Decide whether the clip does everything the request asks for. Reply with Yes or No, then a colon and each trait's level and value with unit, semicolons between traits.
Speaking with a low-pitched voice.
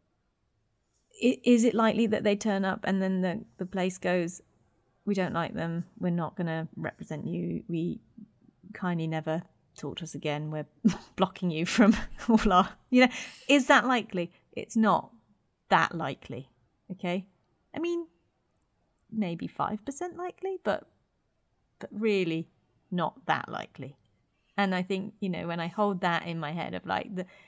No: medium, 185 Hz